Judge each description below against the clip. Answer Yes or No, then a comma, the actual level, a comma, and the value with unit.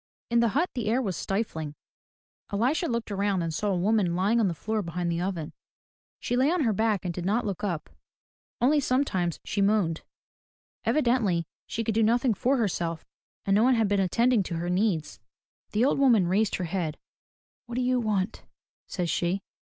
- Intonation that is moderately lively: Yes, average, 4.8 semitones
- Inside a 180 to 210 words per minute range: Yes, average, 190 wpm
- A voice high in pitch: Yes, high, 205 Hz